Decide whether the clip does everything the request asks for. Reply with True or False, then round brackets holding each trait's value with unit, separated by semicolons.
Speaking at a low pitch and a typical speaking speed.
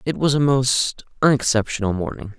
True (125 Hz; 150 wpm)